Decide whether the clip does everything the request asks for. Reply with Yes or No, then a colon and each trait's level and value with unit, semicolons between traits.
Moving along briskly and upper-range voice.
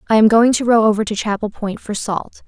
Yes: fast, 265 wpm; high, 215 Hz